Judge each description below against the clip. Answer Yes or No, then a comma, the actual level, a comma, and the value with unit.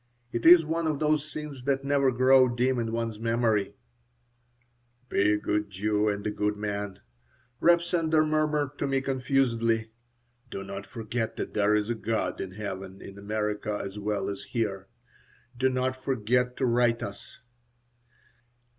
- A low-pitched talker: Yes, low, 115 Hz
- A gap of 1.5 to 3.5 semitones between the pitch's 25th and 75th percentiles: No, average, 4.4 semitones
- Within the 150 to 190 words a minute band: Yes, average, 155 wpm